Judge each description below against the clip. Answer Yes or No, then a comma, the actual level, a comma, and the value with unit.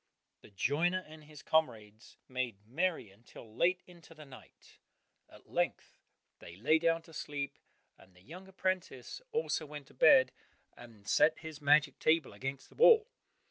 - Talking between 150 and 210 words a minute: Yes, average, 155 wpm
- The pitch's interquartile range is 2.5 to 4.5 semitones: No, wide, 5.6 semitones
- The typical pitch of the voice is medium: Yes, medium, 150 Hz